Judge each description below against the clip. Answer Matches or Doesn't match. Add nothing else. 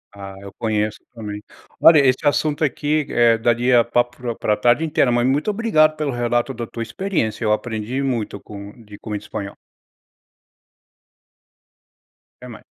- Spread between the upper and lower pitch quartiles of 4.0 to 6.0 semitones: Matches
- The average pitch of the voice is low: Matches